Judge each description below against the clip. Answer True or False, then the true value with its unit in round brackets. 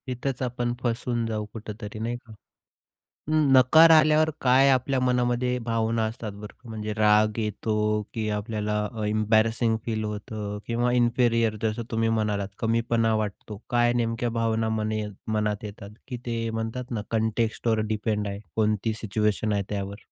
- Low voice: True (115 Hz)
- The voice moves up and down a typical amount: False (2.0 semitones)